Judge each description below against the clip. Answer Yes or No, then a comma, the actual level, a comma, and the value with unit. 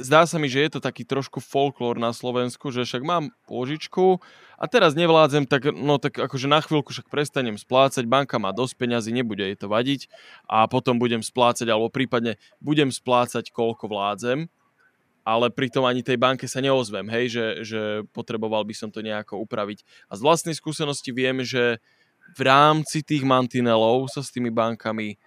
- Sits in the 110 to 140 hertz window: Yes, low, 125 Hz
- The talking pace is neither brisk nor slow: No, fast, 180 wpm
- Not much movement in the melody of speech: No, average, 3.6 semitones